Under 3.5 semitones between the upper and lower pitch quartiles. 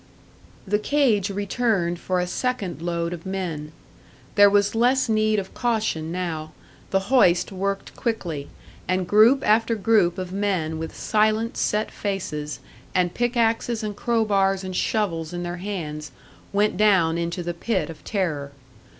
No: average, 4.0 semitones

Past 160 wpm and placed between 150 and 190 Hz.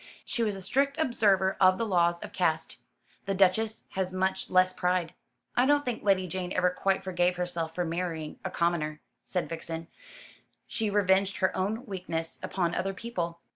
Yes: average, 175 wpm; medium, 185 Hz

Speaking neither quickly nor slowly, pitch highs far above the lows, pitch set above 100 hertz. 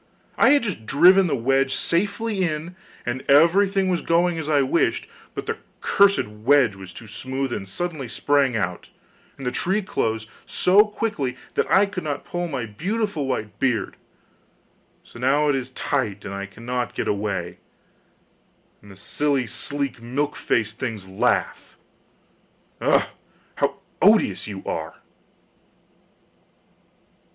Yes: average, 145 wpm; wide, 7.7 semitones; low, 135 Hz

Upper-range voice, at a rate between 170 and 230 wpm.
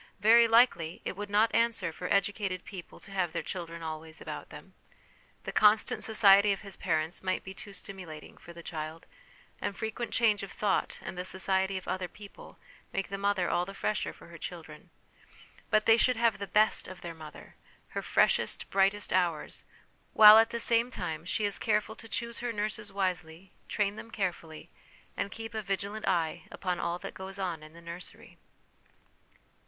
Yes: high, 195 Hz; average, 185 wpm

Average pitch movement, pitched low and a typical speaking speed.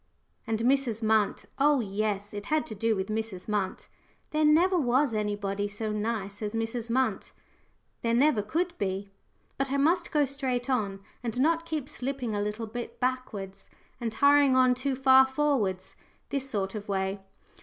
No: average, 4.8 semitones; high, 230 Hz; average, 165 wpm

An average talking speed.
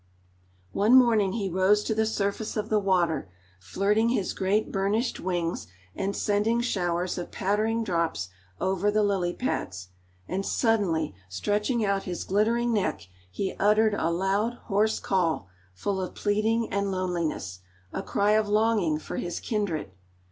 Yes: average, 150 wpm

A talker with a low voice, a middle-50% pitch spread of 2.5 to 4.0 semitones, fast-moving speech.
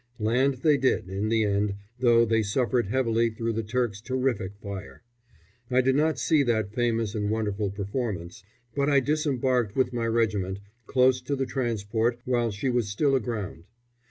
No: low, 115 Hz; average, 3.6 semitones; average, 165 wpm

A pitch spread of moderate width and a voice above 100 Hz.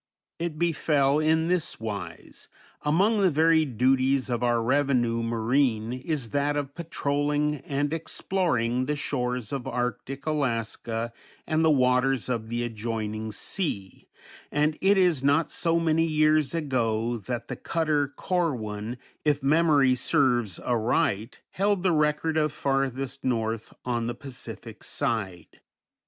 Yes: average, 4.7 semitones; low, 135 Hz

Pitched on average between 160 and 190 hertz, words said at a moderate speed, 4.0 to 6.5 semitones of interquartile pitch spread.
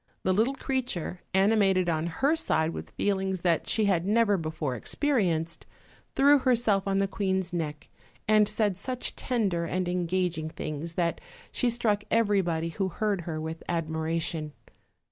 Yes: medium, 185 Hz; average, 155 wpm; average, 4.3 semitones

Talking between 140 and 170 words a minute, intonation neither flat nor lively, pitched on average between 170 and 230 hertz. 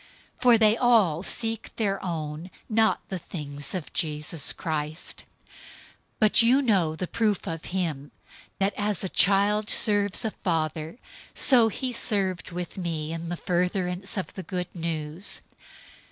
Yes: average, 145 wpm; average, 4.5 semitones; medium, 185 Hz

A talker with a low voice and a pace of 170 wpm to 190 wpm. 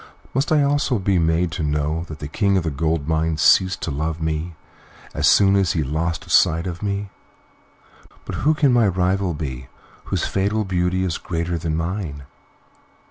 Yes: very low, 85 Hz; average, 180 wpm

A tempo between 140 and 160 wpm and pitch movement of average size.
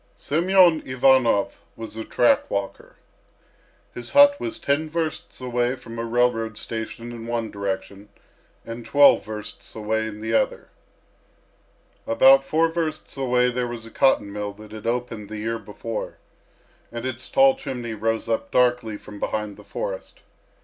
Yes: average, 150 wpm; average, 3.5 semitones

